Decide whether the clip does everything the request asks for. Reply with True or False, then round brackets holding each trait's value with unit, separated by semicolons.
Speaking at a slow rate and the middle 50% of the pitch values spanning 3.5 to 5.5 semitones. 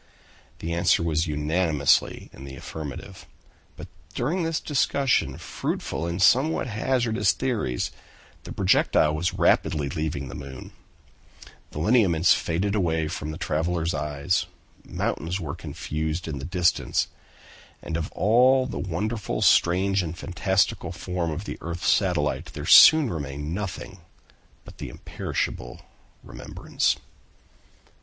True (125 wpm; 4.6 semitones)